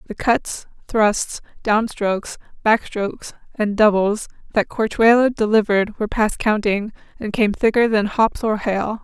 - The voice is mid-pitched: No, high, 215 Hz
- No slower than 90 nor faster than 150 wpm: Yes, average, 145 wpm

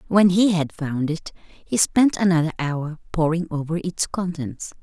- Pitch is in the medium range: Yes, medium, 170 Hz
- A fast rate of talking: No, average, 160 wpm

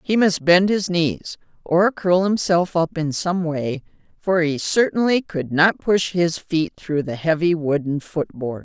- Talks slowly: No, average, 180 wpm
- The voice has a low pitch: No, medium, 170 Hz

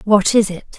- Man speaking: No, female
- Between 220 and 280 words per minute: Yes, fast, 230 wpm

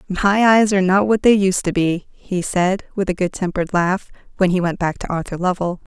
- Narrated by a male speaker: No, female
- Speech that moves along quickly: Yes, fast, 230 wpm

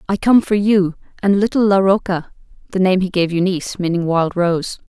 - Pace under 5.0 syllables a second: Yes, 3.3 syllables/s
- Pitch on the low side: No, medium, 185 Hz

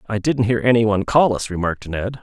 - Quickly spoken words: Yes, fast, 245 wpm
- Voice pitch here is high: No, low, 110 Hz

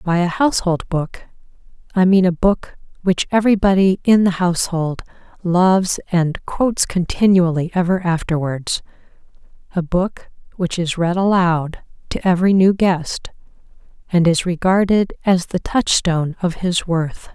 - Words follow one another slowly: Yes, slow, 130 wpm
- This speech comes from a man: No, female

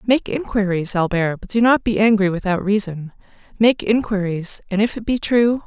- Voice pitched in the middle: No, high, 205 Hz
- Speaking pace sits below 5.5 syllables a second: Yes, 5.0 syllables/s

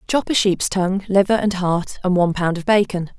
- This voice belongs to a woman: Yes, female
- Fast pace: Yes, fast, 225 wpm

